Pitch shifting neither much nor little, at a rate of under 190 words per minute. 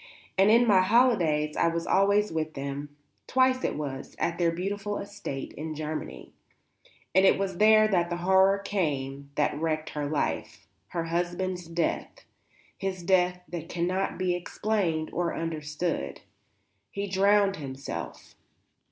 Yes: average, 4.0 semitones; average, 140 wpm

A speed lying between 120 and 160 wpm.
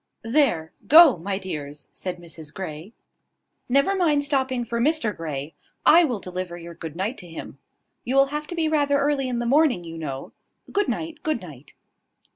No: average, 180 wpm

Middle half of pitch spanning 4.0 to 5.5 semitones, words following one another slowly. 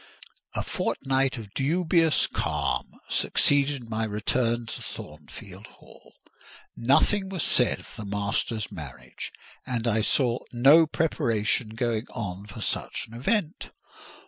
Yes: average, 4.5 semitones; slow, 120 wpm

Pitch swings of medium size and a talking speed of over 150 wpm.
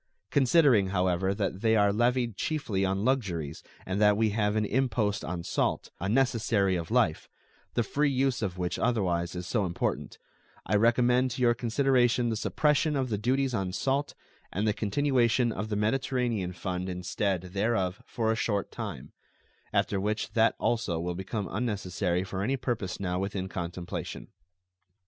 Yes: average, 4.5 semitones; average, 165 wpm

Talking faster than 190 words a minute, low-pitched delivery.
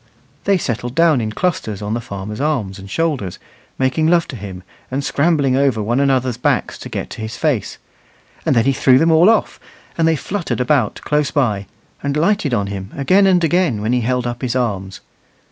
Yes: average, 200 wpm; low, 130 Hz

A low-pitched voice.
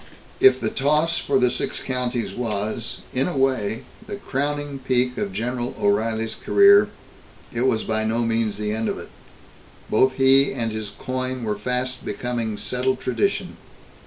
Yes: low, 125 Hz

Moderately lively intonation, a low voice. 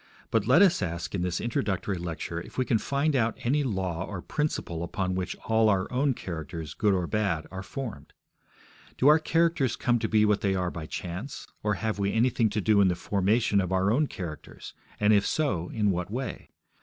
Yes: average, 4.7 semitones; low, 105 Hz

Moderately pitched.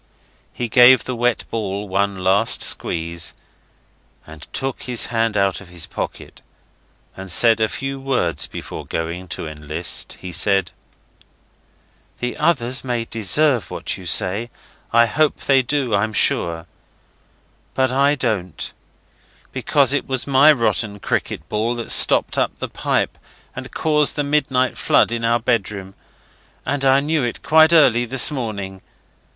No: low, 115 Hz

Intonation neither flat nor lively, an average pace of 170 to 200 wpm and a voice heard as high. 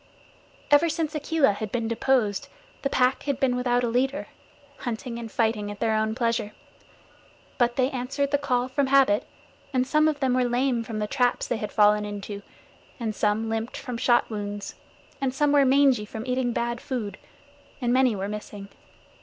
Yes: average, 3.5 semitones; average, 180 wpm; high, 245 Hz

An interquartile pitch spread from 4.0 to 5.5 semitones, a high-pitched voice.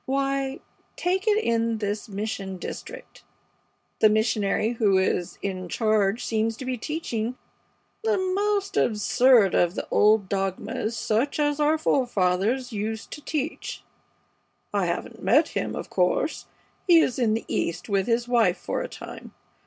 Yes: average, 5.1 semitones; high, 225 Hz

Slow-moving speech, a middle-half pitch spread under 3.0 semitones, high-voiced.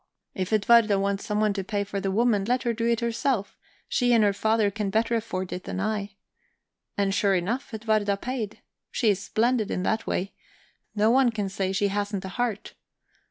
No: average, 190 wpm; narrow, 2.5 semitones; high, 210 Hz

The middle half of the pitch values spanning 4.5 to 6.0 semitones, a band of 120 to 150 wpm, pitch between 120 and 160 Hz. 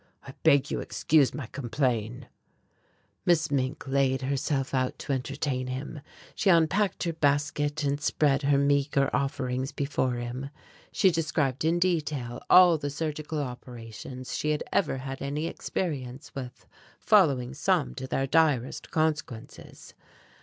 No: average, 3.0 semitones; slow, 135 wpm; medium, 140 Hz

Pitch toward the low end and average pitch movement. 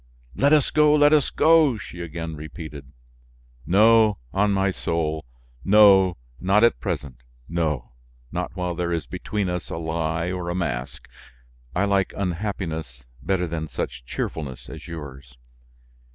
Yes: very low, 90 Hz; average, 4.2 semitones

